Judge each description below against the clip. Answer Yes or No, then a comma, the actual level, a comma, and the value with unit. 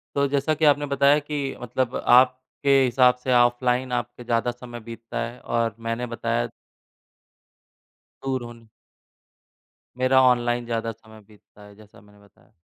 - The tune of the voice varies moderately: No, narrow, 2.2 semitones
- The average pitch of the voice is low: Yes, low, 120 Hz